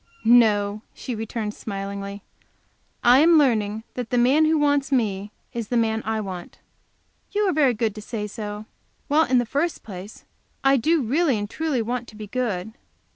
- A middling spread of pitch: Yes, average, 4.5 semitones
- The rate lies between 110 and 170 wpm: No, average, 180 wpm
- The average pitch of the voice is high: Yes, high, 230 Hz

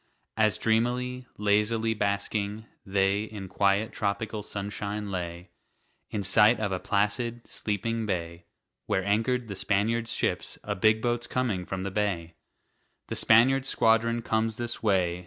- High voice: No, low, 105 Hz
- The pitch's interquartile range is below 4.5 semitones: Yes, narrow, 2.6 semitones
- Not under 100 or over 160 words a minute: Yes, average, 140 wpm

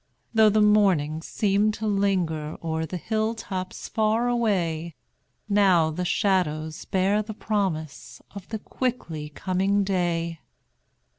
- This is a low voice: No, high, 190 Hz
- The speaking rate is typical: No, slow, 125 wpm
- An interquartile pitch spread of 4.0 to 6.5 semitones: Yes, average, 4.4 semitones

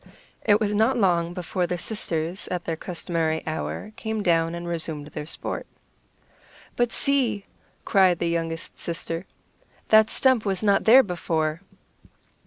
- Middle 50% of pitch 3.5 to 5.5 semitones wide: Yes, average, 4.3 semitones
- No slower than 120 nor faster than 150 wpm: Yes, average, 140 wpm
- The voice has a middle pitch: Yes, medium, 180 Hz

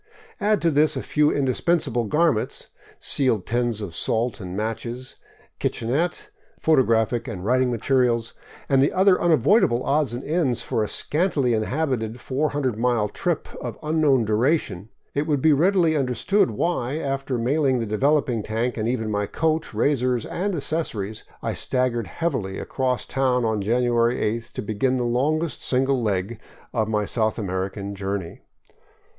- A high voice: No, low, 125 Hz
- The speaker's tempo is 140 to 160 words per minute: Yes, average, 150 wpm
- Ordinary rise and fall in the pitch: Yes, average, 4.8 semitones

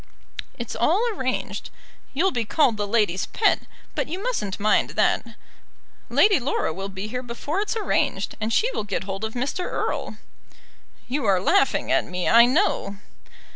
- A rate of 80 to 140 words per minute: No, average, 165 wpm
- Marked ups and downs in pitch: Yes, wide, 8.8 semitones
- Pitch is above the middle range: Yes, high, 235 Hz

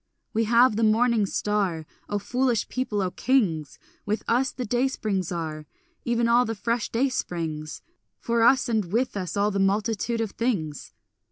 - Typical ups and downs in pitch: Yes, average, 3.7 semitones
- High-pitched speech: Yes, high, 220 Hz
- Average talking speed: Yes, average, 170 wpm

